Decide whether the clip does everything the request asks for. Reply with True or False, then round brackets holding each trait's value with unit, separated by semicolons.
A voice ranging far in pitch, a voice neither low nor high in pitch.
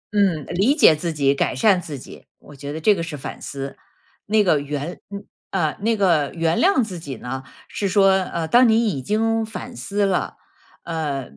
True (6.0 semitones; 175 Hz)